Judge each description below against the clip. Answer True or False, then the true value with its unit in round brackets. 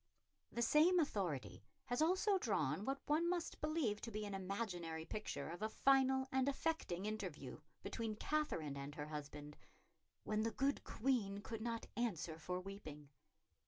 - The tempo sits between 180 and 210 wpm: False (155 wpm)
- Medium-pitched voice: False (215 Hz)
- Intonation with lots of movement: True (7.8 semitones)